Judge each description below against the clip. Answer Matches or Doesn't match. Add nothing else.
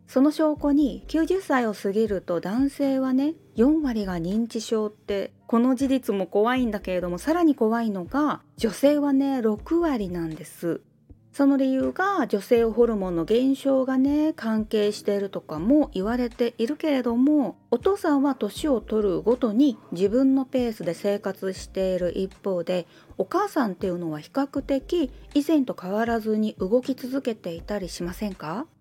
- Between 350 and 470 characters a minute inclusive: Doesn't match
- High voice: Matches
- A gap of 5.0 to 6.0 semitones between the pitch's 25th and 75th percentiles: Matches